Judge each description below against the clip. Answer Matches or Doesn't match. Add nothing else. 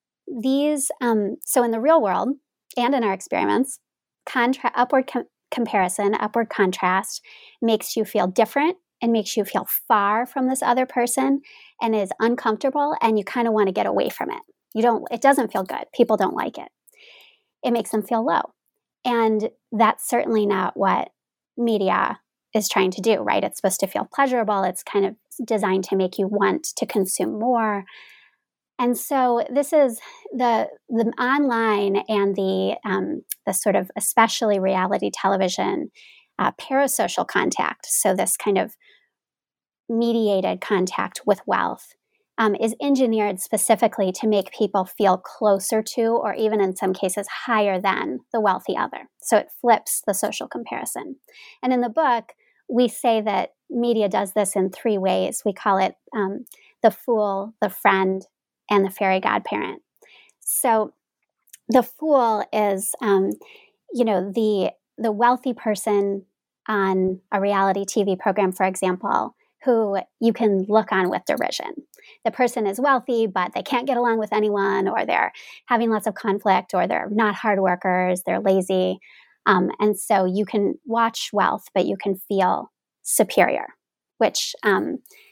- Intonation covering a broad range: Doesn't match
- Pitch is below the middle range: Doesn't match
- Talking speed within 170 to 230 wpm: Doesn't match